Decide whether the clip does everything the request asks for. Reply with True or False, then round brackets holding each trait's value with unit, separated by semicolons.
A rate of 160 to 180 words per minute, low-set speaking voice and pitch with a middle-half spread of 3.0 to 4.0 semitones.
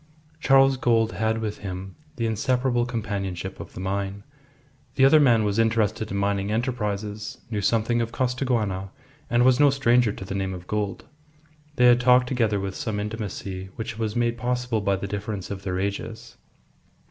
True (170 wpm; 110 Hz; 3.4 semitones)